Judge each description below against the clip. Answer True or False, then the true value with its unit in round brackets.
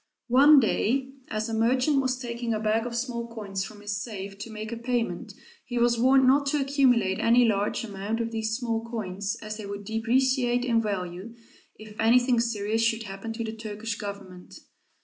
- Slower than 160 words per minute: False (190 wpm)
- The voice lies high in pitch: True (225 Hz)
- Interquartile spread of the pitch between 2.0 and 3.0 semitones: True (2.6 semitones)